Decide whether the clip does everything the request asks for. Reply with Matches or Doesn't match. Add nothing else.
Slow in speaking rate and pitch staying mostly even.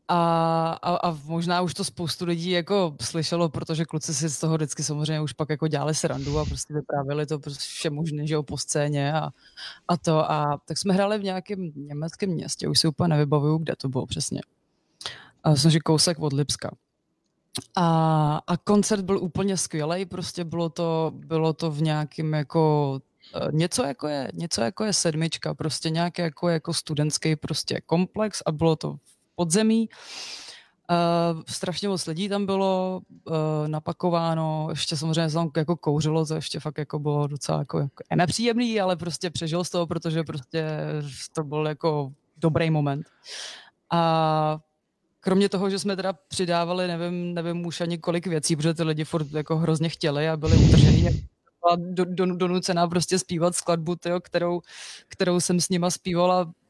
Doesn't match